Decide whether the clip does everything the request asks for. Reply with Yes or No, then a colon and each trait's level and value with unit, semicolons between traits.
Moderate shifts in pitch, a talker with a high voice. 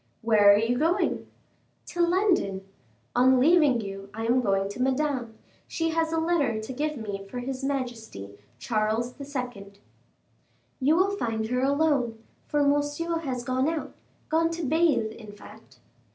No: wide, 5.7 semitones; very high, 255 Hz